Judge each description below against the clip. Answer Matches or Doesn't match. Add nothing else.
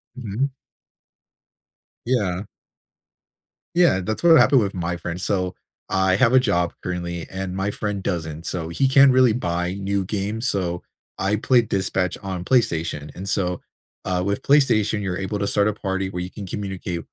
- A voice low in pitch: Matches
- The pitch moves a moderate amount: Matches